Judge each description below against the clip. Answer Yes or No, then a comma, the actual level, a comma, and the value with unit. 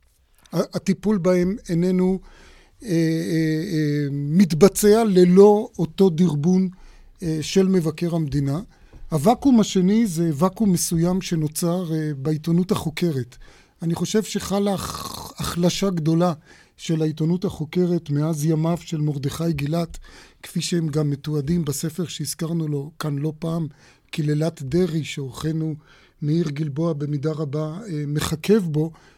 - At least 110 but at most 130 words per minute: Yes, average, 115 wpm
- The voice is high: No, medium, 165 Hz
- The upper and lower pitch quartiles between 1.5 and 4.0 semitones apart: Yes, average, 2.9 semitones